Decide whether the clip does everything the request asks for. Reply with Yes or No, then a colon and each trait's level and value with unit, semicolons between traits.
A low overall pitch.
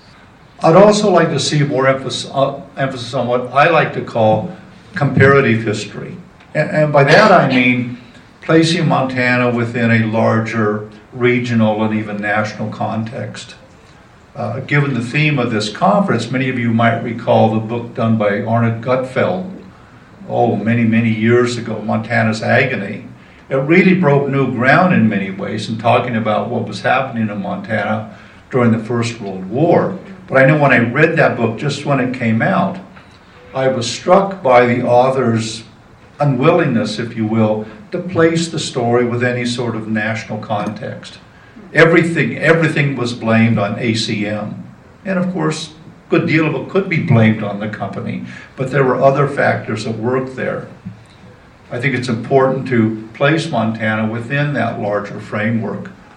Yes: low, 120 Hz